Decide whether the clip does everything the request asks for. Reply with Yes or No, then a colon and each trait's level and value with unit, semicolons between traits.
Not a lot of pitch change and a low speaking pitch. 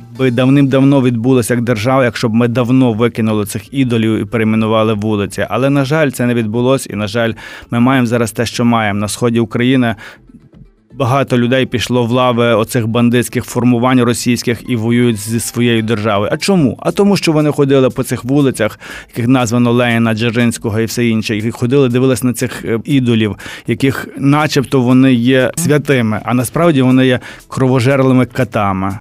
Yes: narrow, 2.2 semitones; low, 120 Hz